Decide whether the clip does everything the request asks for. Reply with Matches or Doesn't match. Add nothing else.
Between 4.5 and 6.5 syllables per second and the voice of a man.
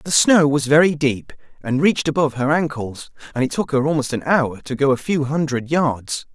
Matches